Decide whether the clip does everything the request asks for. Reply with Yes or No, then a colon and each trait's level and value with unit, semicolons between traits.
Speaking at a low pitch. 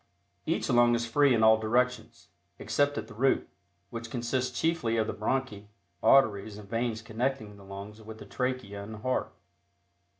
Yes: low, 115 Hz